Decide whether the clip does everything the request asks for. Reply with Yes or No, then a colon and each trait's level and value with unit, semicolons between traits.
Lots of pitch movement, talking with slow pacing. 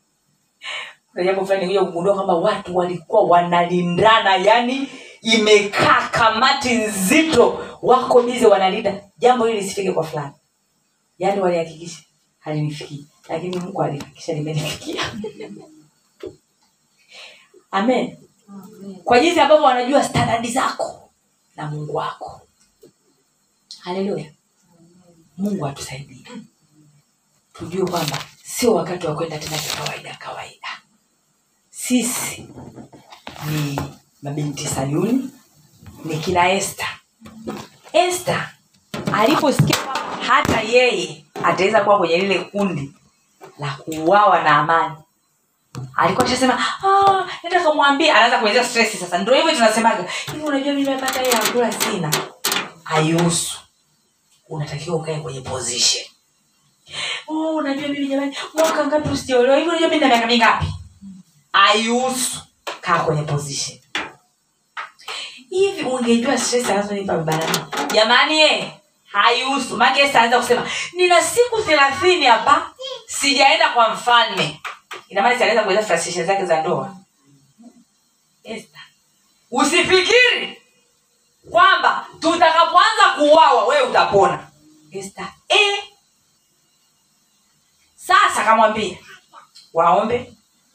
Yes: wide, 8.0 semitones; slow, 55 wpm